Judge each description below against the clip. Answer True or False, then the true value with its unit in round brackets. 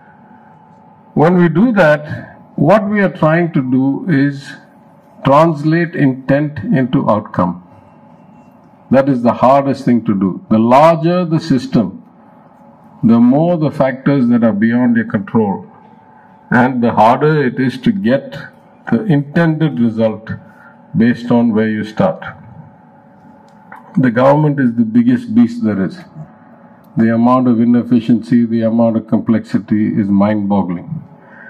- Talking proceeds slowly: True (130 wpm)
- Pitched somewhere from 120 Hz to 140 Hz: True (135 Hz)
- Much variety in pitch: True (7.2 semitones)